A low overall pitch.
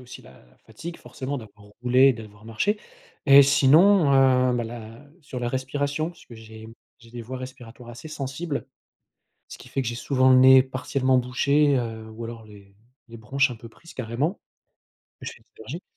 Yes: low, 130 Hz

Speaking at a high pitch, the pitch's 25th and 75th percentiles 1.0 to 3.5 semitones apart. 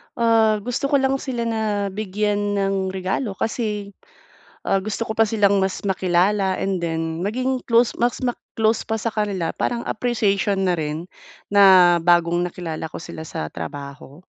No: high, 200 Hz; average, 3.9 semitones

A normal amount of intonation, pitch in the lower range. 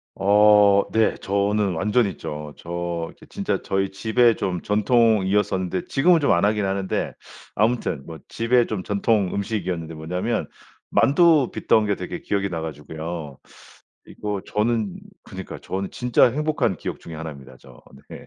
Yes: average, 4.3 semitones; low, 100 Hz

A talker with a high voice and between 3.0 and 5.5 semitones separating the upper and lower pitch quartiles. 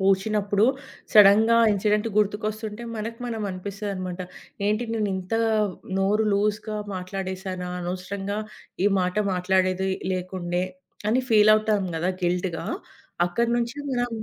No: high, 200 Hz; narrow, 2.5 semitones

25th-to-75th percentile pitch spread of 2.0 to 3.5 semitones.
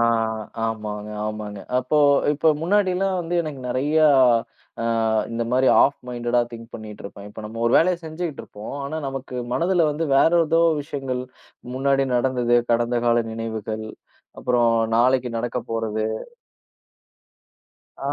No: average, 4.2 semitones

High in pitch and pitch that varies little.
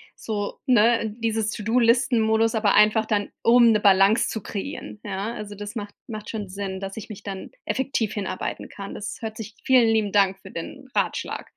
Yes: high, 215 Hz; narrow, 2.0 semitones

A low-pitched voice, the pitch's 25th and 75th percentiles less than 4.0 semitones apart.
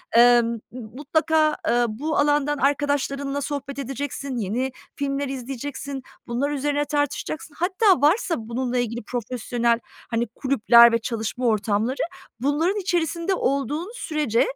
No: very high, 275 Hz; average, 3.6 semitones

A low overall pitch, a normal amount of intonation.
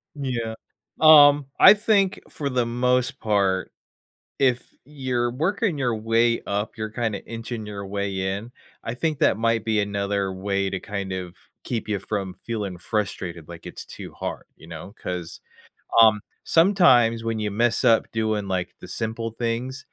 Yes: low, 115 Hz; average, 3.8 semitones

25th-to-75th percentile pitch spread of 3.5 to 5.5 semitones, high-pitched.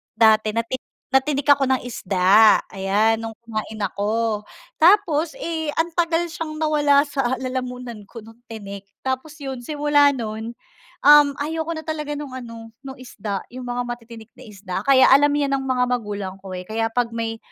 Yes: average, 4.7 semitones; high, 245 Hz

